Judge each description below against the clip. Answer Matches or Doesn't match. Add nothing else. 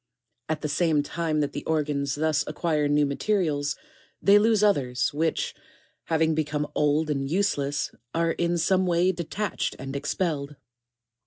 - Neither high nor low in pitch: Matches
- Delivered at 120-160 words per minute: Matches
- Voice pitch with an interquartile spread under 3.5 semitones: Matches